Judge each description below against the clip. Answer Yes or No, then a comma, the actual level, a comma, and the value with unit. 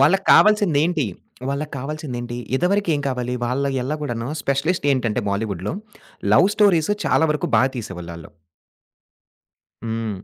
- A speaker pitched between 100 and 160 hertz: Yes, low, 135 Hz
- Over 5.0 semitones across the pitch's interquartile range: Yes, wide, 5.6 semitones